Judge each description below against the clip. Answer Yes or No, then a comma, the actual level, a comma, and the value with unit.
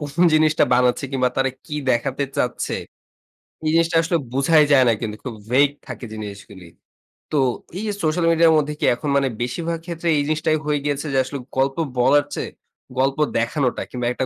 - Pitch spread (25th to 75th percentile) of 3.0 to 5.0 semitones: Yes, average, 3.8 semitones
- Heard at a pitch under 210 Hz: Yes, medium, 140 Hz